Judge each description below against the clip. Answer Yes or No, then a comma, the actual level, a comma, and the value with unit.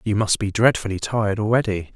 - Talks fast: No, average, 185 wpm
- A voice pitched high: No, low, 105 Hz